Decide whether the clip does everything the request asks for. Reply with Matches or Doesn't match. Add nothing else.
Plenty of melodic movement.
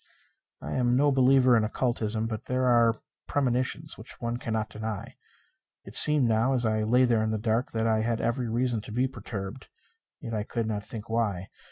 Doesn't match